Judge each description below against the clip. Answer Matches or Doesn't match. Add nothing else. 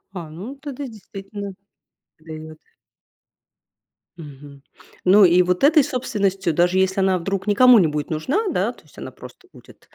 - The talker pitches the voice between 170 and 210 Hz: Matches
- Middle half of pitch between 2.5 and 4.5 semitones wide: Doesn't match